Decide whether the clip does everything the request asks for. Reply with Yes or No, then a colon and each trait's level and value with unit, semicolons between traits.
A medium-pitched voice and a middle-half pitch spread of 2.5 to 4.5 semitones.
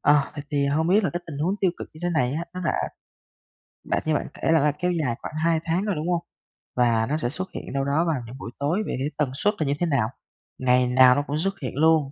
Yes: medium, 150 Hz; average, 3.8 semitones